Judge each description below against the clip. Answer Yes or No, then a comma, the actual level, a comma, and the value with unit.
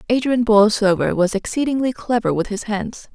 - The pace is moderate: Yes, average, 150 wpm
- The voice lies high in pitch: Yes, high, 220 Hz